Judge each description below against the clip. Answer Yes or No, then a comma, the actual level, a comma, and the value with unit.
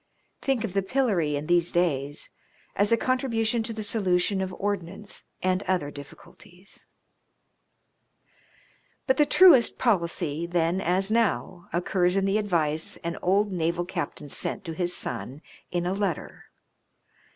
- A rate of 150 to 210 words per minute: No, average, 140 wpm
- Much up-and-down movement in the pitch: No, average, 3.6 semitones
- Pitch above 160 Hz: Yes, medium, 185 Hz